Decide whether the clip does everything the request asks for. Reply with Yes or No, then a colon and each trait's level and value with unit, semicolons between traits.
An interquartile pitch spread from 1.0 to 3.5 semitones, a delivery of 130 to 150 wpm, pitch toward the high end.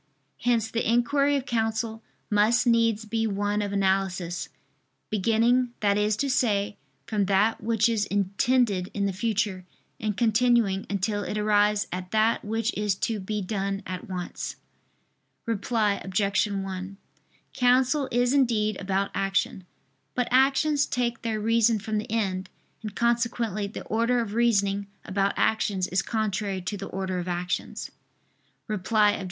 Yes: average, 2.8 semitones; average, 145 wpm; high, 210 Hz